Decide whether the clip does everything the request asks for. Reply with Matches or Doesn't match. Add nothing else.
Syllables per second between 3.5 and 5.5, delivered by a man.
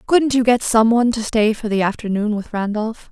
Doesn't match